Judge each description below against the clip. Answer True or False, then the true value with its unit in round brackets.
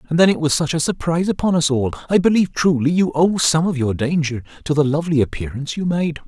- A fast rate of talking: True (230 wpm)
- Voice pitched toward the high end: False (155 Hz)